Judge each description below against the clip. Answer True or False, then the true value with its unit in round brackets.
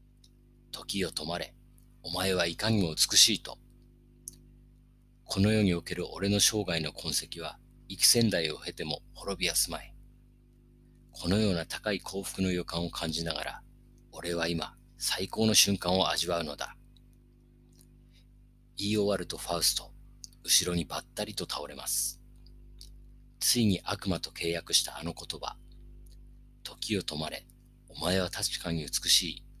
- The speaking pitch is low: True (90 Hz)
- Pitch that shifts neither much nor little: True (3.3 semitones)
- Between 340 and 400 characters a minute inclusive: False (255 characters per minute)